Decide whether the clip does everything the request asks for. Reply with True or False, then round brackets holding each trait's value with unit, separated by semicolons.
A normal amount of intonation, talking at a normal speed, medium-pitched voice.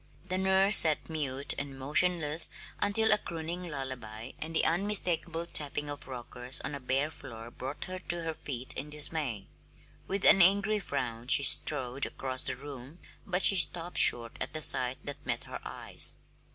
True (4.9 semitones; 170 wpm; 150 Hz)